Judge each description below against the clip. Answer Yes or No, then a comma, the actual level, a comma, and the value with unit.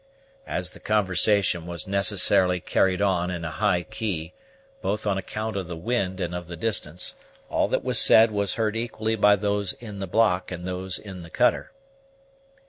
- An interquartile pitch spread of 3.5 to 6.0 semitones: No, average, 3.0 semitones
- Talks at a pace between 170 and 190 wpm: Yes, average, 180 wpm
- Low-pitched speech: Yes, very low, 95 Hz